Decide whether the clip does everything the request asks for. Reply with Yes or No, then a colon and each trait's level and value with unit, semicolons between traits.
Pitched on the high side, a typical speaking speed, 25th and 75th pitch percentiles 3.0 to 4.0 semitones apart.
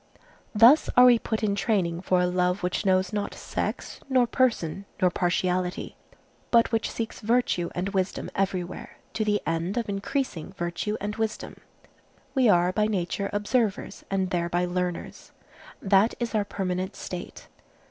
Yes: high, 195 Hz; average, 150 wpm; average, 3.4 semitones